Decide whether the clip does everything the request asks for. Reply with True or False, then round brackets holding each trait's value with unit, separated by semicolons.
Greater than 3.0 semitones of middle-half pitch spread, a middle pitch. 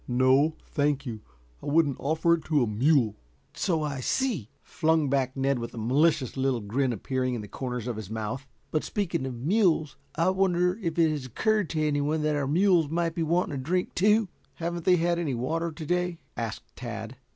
True (4.7 semitones; 150 Hz)